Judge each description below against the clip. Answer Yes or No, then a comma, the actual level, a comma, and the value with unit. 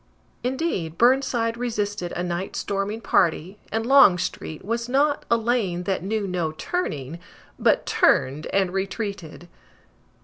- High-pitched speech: Yes, high, 200 Hz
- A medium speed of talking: No, slow, 125 wpm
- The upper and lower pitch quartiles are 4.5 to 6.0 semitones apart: Yes, average, 5.0 semitones